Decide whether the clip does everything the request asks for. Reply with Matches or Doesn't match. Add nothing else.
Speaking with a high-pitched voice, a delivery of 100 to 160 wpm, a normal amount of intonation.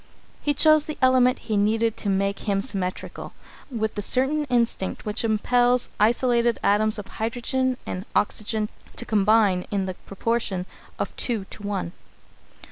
Matches